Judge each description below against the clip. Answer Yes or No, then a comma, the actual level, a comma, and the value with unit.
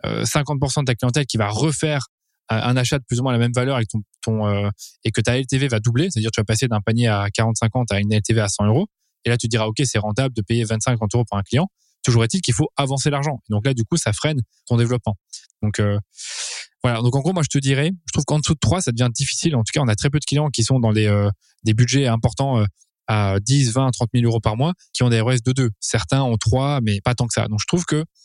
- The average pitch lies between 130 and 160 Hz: No, low, 120 Hz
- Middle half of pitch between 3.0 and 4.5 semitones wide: Yes, average, 3.8 semitones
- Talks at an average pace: No, fast, 285 wpm